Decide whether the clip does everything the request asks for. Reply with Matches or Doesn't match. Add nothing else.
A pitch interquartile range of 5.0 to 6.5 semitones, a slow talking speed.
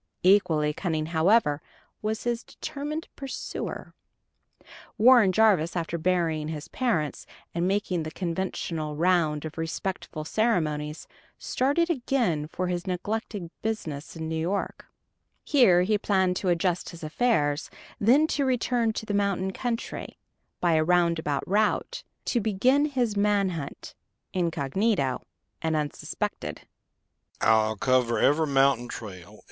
Matches